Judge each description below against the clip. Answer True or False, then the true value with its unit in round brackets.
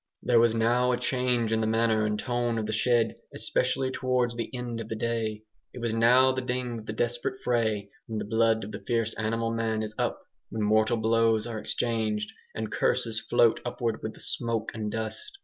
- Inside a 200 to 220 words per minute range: True (205 wpm)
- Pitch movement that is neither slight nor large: False (1.6 semitones)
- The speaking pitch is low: True (115 Hz)